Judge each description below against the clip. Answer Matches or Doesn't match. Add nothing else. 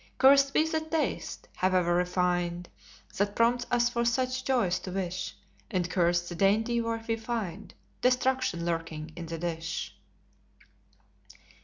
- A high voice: Matches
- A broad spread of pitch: Matches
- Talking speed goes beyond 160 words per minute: Doesn't match